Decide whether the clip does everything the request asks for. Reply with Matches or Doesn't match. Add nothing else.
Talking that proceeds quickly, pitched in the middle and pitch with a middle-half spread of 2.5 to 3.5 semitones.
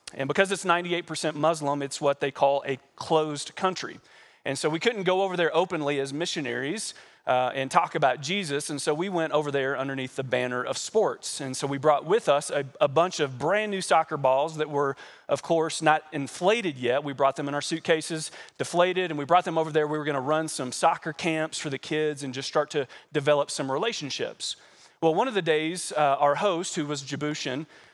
Matches